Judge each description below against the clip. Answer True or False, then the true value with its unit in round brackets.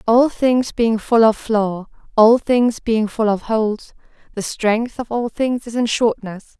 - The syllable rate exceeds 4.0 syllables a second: False (3.8 syllables/s)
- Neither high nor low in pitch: False (225 Hz)